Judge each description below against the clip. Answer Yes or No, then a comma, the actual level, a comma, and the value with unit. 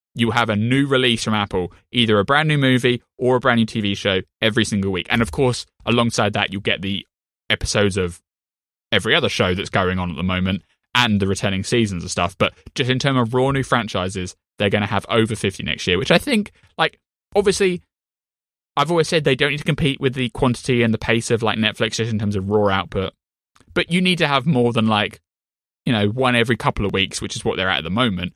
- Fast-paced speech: Yes, fast, 240 wpm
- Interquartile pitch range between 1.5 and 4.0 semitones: No, average, 4.6 semitones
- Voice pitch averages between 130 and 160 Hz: No, low, 110 Hz